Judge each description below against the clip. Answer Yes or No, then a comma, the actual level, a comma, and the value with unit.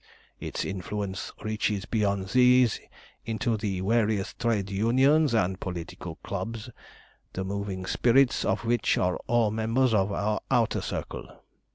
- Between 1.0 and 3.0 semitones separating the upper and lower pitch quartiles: No, average, 3.4 semitones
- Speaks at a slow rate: Yes, slow, 130 wpm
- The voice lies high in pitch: No, low, 105 Hz